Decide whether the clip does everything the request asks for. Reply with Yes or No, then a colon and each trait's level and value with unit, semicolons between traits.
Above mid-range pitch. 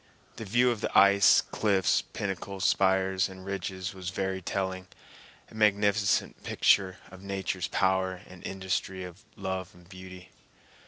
No: very low, 95 Hz